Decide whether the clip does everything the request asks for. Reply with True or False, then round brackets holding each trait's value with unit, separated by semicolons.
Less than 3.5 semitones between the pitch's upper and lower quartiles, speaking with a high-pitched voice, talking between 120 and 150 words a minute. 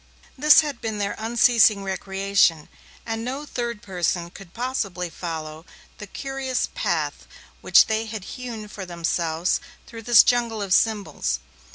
False (4.5 semitones; 215 Hz; 140 wpm)